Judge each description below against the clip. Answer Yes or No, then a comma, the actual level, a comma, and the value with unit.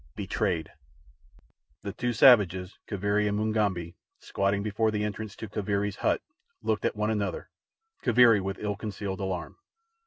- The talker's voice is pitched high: No, low, 105 Hz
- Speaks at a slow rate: Yes, slow, 130 wpm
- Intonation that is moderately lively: No, narrow, 1.8 semitones